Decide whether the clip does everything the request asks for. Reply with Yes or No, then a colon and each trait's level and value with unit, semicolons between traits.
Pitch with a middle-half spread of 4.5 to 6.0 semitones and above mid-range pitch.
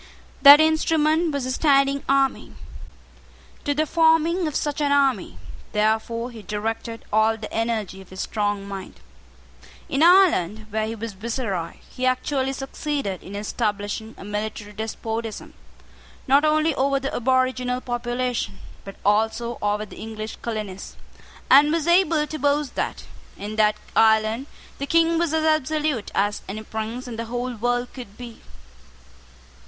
Yes: average, 4.8 semitones; high, 240 Hz